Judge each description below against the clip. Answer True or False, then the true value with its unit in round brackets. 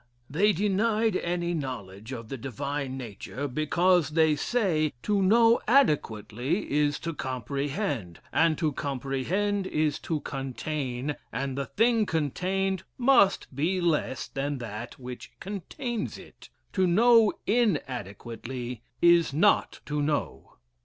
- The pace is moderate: False (120 wpm)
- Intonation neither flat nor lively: False (6.5 semitones)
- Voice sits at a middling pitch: True (150 Hz)